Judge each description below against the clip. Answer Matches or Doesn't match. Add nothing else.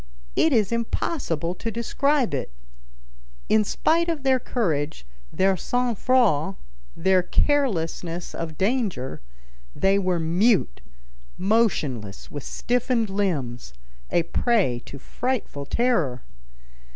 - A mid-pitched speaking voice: Doesn't match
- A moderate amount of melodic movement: Doesn't match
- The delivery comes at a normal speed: Doesn't match